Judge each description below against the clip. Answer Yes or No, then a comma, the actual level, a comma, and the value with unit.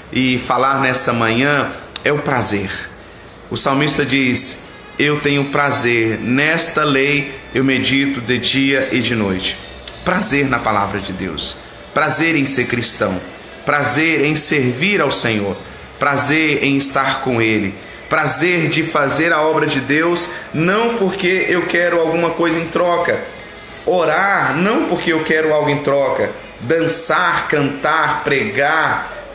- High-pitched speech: No, medium, 140 Hz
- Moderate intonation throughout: Yes, average, 4.3 semitones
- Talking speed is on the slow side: No, average, 135 wpm